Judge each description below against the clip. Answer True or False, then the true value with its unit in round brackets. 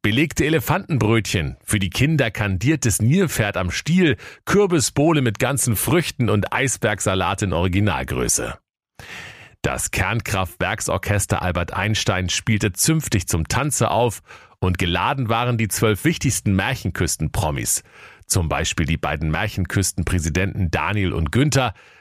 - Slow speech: True (110 wpm)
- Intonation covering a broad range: True (6.0 semitones)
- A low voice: True (110 Hz)